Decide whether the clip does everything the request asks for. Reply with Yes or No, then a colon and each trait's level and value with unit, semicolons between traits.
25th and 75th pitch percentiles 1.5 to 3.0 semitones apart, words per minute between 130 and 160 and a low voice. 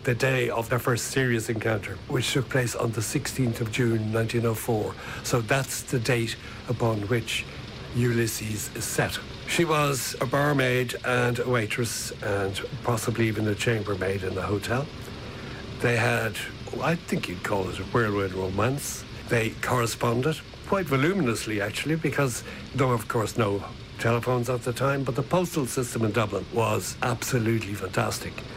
Yes: narrow, 2.6 semitones; average, 155 wpm; low, 120 Hz